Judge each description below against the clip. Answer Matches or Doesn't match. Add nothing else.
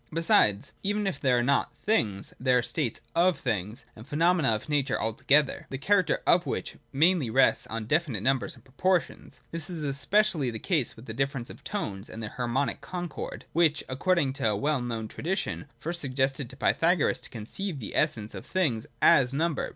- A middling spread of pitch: Doesn't match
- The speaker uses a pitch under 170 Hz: Matches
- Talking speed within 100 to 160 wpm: Doesn't match